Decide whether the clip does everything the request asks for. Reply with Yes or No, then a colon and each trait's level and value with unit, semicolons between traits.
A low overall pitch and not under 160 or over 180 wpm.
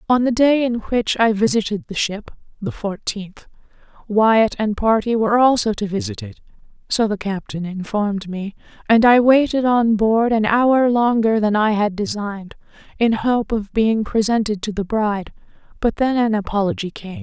No: high, 220 Hz; average, 165 wpm